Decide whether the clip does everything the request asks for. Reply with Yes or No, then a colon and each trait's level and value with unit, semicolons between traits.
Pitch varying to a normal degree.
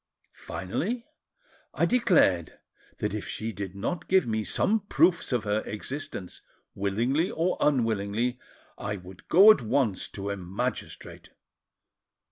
No: wide, 8.4 semitones